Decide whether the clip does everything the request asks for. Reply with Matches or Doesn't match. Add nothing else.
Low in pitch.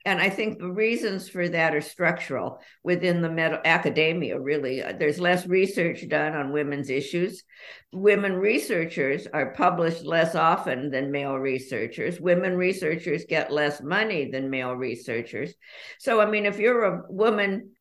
Doesn't match